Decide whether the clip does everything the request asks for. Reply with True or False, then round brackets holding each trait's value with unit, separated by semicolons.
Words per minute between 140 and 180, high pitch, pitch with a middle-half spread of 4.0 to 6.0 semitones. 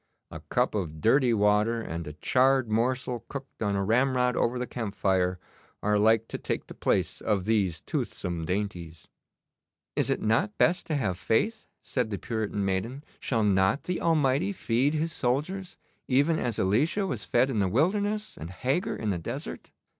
False (175 wpm; 115 Hz; 5.4 semitones)